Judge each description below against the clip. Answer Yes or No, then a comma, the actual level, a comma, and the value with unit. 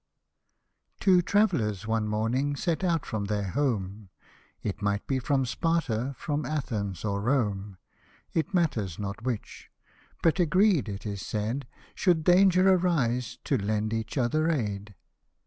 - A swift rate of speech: No, slow, 135 wpm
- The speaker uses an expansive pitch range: Yes, wide, 7.3 semitones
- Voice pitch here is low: Yes, low, 120 Hz